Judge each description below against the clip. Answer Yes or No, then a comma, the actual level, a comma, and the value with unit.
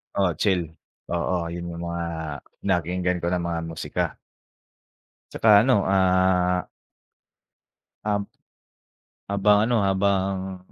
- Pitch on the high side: No, very low, 95 Hz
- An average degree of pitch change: No, narrow, 2.1 semitones